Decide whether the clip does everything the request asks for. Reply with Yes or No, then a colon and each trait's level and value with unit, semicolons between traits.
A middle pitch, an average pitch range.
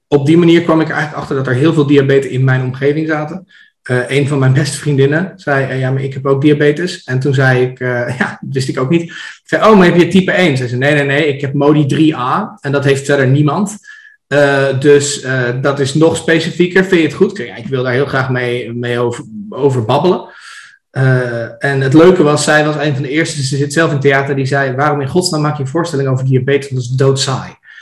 Yes: medium, 145 Hz; average, 3.4 semitones